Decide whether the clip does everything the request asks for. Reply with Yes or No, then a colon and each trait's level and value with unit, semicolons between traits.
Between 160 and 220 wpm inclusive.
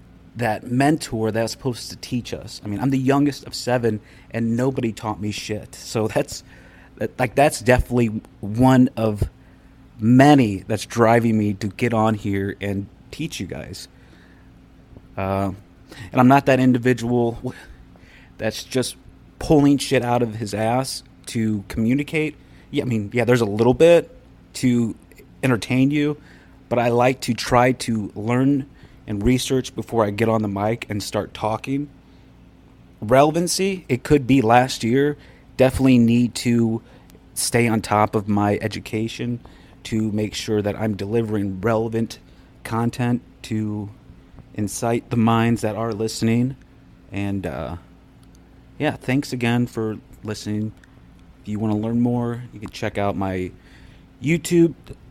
No: average, 145 wpm